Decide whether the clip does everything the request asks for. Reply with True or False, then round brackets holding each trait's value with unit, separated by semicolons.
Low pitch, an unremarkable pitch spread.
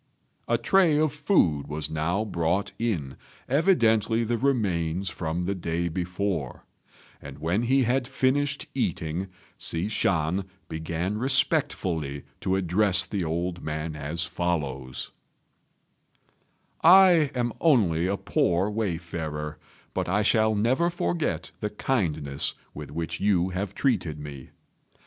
False (90 Hz; 6.4 semitones)